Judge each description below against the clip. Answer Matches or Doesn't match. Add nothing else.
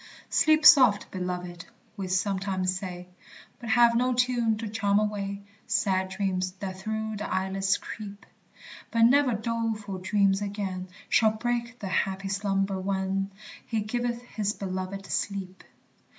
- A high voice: Matches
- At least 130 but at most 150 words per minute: Matches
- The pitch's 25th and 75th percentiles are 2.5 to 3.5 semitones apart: Matches